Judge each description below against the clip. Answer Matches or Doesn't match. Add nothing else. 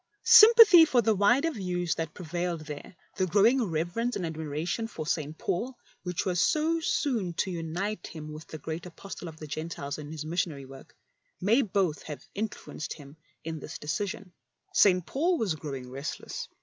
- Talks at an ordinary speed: Matches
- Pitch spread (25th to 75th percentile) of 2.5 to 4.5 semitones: Doesn't match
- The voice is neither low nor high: Matches